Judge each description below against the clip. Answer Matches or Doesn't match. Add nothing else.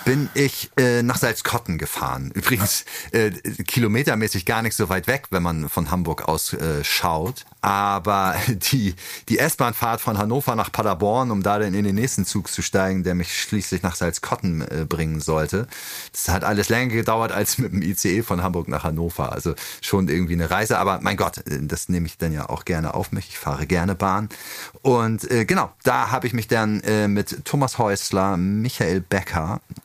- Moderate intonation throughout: Matches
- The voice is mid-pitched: Doesn't match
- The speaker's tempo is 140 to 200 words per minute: Matches